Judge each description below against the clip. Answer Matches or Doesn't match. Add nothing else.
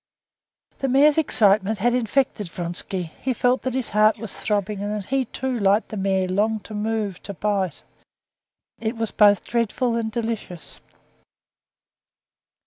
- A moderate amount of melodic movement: Matches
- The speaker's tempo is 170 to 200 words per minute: Doesn't match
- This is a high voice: Matches